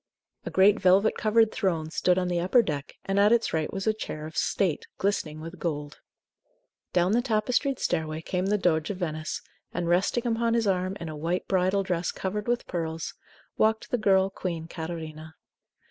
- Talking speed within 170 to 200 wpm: Yes, average, 185 wpm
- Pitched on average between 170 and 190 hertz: Yes, medium, 185 Hz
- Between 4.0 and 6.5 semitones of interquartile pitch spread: Yes, average, 4.3 semitones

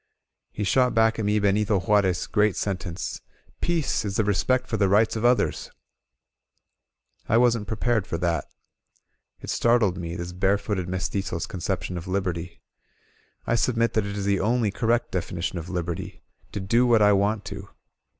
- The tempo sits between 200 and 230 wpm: No, average, 170 wpm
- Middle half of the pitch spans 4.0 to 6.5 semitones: No, average, 3.4 semitones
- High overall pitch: No, low, 100 Hz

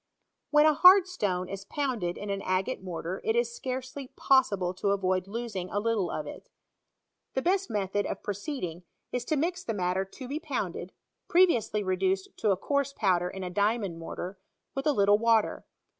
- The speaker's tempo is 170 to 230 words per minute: Yes, average, 185 wpm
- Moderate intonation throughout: No, wide, 6.4 semitones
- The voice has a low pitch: No, high, 205 Hz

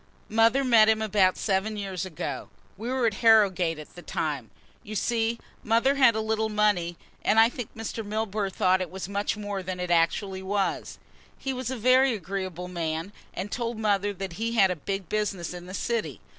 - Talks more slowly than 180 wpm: No, average, 195 wpm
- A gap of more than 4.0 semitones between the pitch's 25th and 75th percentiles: No, average, 3.3 semitones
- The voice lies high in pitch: Yes, high, 205 Hz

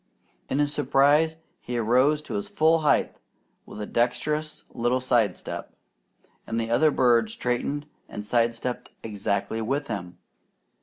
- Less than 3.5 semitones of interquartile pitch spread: No, average, 4.5 semitones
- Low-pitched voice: Yes, low, 125 Hz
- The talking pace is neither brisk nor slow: Yes, average, 145 wpm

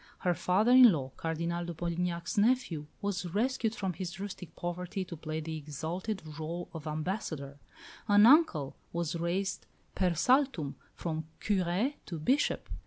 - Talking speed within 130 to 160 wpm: Yes, average, 145 wpm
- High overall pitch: No, medium, 175 Hz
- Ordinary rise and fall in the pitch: Yes, average, 4.2 semitones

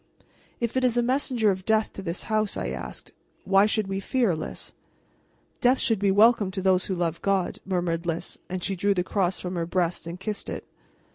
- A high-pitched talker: Yes, high, 195 Hz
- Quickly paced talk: Yes, fast, 210 wpm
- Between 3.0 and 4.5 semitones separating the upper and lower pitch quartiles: Yes, average, 3.3 semitones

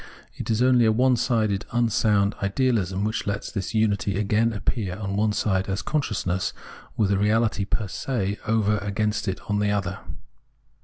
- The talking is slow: No, average, 160 wpm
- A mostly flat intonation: Yes, narrow, 2.0 semitones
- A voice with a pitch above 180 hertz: No, low, 105 Hz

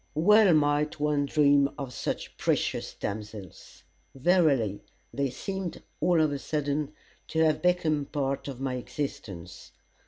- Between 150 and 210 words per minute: No, slow, 135 wpm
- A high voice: No, medium, 145 Hz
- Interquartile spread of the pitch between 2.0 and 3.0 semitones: Yes, average, 2.7 semitones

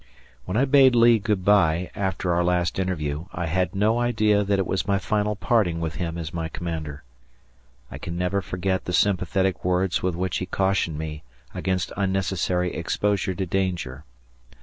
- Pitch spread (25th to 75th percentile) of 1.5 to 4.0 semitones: Yes, narrow, 2.6 semitones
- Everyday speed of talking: Yes, average, 170 wpm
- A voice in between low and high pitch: No, very low, 95 Hz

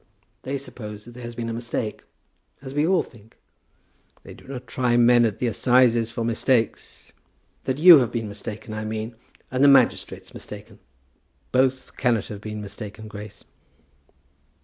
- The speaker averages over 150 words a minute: Yes, average, 160 wpm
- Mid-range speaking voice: No, low, 120 Hz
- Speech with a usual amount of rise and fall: Yes, average, 3.0 semitones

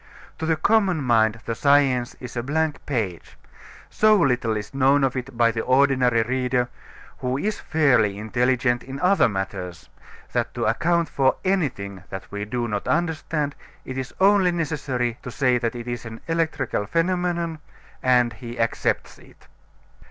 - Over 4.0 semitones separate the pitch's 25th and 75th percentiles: Yes, average, 5.2 semitones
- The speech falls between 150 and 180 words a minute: Yes, average, 160 wpm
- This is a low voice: Yes, low, 130 Hz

